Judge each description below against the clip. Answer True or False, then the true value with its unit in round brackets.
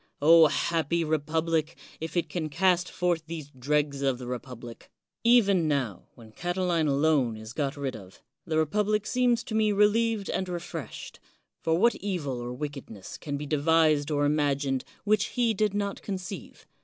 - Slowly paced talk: False (155 wpm)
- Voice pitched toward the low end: False (160 Hz)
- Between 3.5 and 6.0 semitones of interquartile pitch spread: True (5.2 semitones)